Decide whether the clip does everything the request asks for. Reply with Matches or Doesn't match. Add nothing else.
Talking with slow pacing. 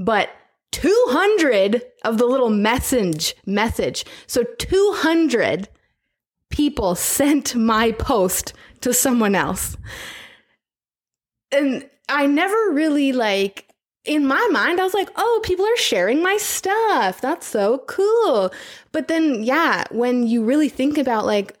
Matches